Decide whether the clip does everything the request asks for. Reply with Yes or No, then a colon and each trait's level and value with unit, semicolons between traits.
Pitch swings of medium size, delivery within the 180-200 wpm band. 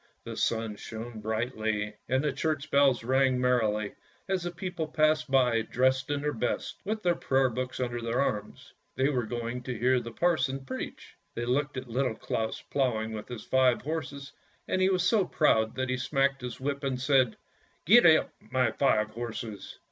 Yes: average, 3.4 semitones; average, 185 wpm